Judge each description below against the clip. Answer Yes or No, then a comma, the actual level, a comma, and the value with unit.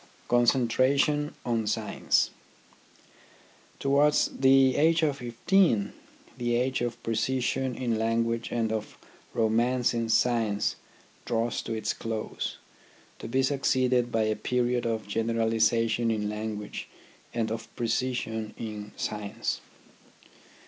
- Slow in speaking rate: Yes, slow, 115 wpm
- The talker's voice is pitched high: No, low, 115 Hz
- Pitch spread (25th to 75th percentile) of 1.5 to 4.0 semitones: Yes, narrow, 2.5 semitones